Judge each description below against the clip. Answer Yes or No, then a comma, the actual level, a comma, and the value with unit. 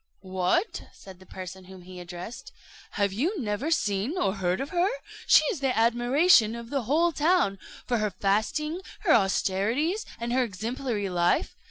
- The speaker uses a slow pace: No, average, 165 wpm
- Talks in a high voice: Yes, high, 230 Hz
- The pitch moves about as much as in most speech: No, wide, 7.2 semitones